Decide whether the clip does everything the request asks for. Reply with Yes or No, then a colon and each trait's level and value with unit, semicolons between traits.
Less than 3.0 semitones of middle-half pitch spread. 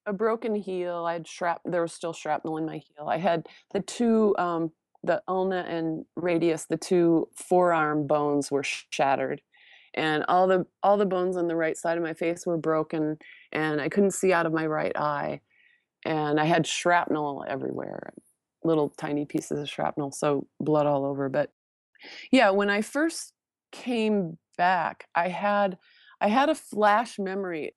No: average, 3.6 semitones